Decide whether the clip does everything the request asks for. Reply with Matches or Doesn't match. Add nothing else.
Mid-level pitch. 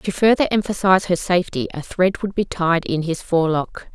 Matches